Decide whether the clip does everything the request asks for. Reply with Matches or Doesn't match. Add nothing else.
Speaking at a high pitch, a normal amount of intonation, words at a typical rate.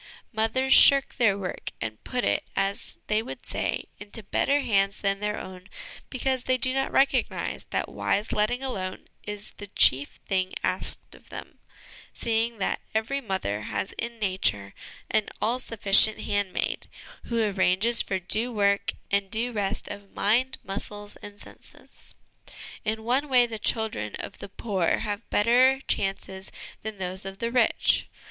Matches